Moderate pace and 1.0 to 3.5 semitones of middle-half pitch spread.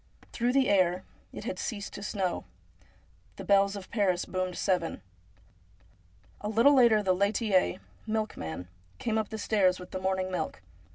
Yes: average, 165 wpm; average, 2.8 semitones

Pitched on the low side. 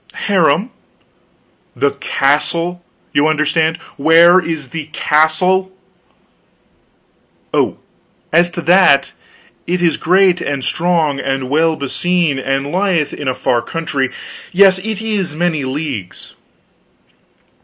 No: medium, 160 Hz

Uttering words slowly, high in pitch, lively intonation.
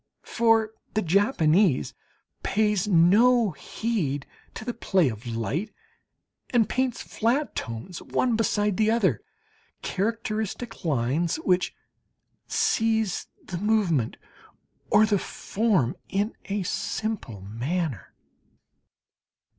Yes: slow, 100 wpm; high, 205 Hz; wide, 5.7 semitones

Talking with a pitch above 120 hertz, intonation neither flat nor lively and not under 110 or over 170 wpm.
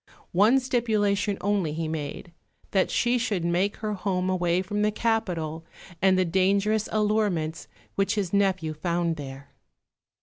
Yes: high, 190 Hz; average, 3.6 semitones; average, 140 wpm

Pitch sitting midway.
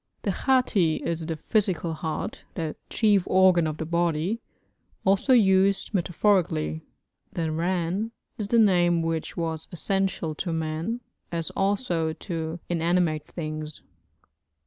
Yes: medium, 170 Hz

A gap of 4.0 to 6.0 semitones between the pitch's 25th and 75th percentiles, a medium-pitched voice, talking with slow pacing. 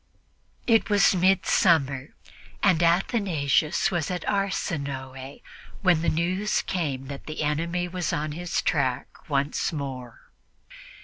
Yes: average, 4.4 semitones; medium, 165 Hz; slow, 115 wpm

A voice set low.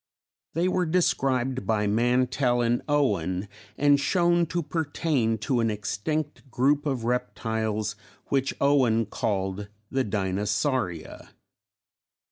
Yes: low, 125 Hz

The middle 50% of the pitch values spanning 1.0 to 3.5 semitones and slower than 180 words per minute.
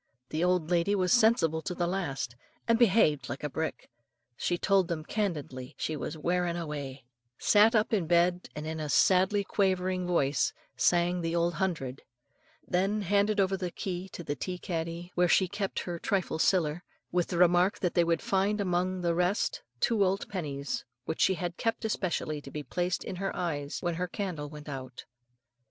No: average, 3.1 semitones; average, 185 wpm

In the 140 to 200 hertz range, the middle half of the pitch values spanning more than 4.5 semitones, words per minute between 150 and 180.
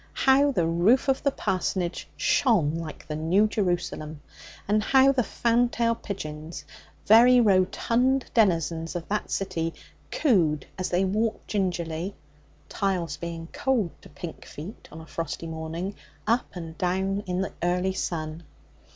No: medium, 185 Hz; average, 5.2 semitones; average, 140 wpm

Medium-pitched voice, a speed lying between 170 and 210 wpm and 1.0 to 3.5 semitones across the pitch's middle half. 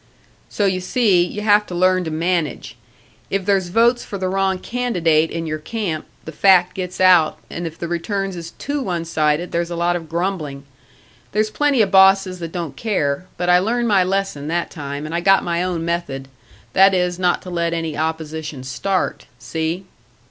Yes: medium, 175 Hz; average, 190 wpm; average, 3.0 semitones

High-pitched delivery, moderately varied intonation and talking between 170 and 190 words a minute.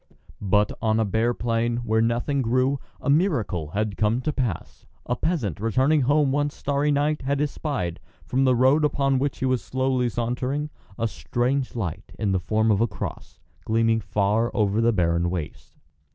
No: low, 120 Hz; average, 4.2 semitones; average, 175 wpm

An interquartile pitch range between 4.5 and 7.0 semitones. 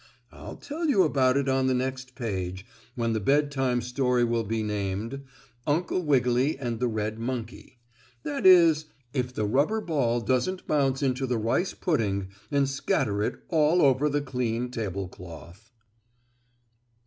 No: average, 4.1 semitones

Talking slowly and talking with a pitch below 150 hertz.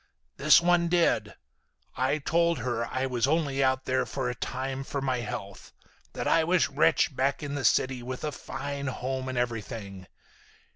No: average, 175 wpm; low, 135 Hz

